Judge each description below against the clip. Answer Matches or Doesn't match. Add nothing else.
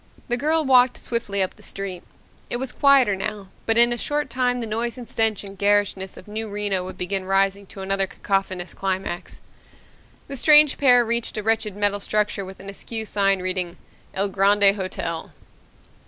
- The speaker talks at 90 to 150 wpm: Doesn't match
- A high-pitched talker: Matches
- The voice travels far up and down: Doesn't match